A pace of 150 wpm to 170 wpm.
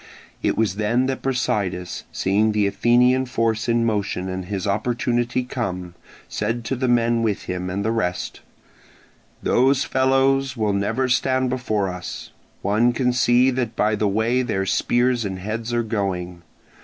Yes: average, 155 wpm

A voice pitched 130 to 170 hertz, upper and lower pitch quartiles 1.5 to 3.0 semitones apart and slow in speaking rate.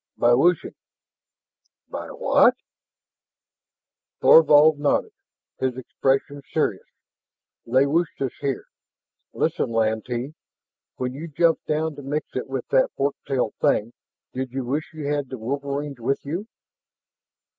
Yes: medium, 140 Hz; average, 2.7 semitones; slow, 125 wpm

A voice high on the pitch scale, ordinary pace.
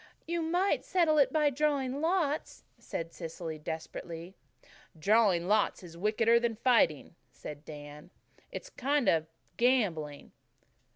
No: high, 220 Hz; slow, 125 wpm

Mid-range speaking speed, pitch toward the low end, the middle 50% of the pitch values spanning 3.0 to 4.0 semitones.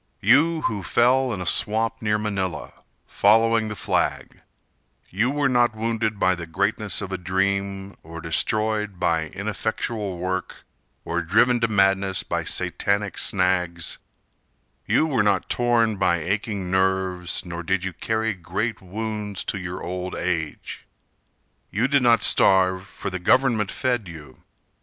Yes: average, 145 wpm; low, 100 Hz; average, 3.3 semitones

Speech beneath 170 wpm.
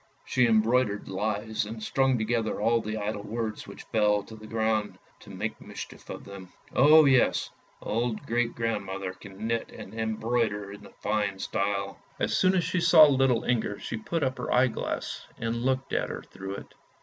No: average, 185 wpm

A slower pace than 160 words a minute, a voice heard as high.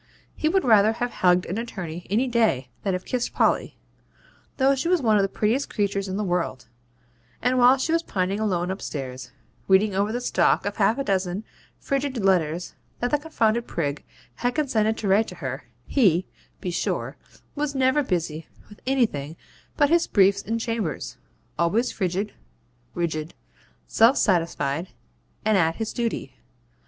No: average, 165 wpm; high, 205 Hz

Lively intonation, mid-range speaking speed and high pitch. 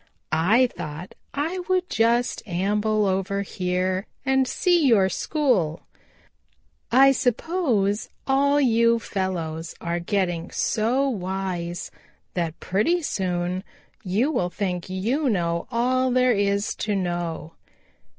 No: wide, 6.0 semitones; slow, 110 wpm; high, 200 Hz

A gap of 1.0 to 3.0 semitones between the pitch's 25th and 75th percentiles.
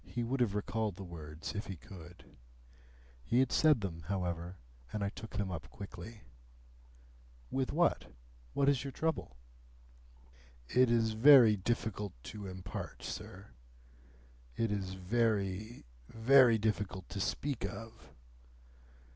No: average, 4.0 semitones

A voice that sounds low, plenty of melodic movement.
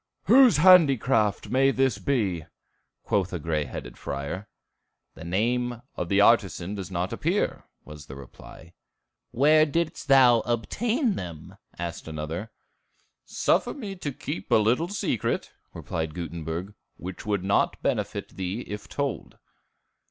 Yes: low, 105 Hz; wide, 7.9 semitones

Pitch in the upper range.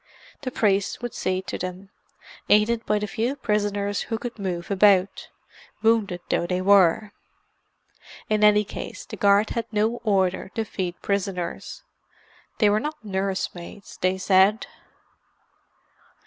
Yes: high, 205 Hz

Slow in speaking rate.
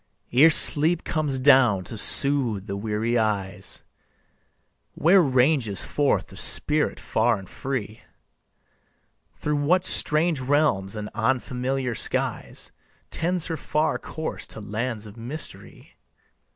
Yes: slow, 115 wpm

